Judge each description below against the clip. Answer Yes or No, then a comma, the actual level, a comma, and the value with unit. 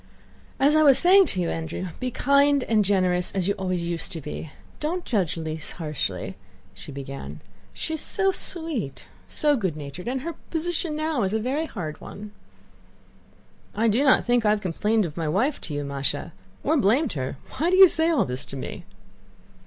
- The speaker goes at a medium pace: Yes, average, 190 wpm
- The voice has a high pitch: Yes, high, 210 Hz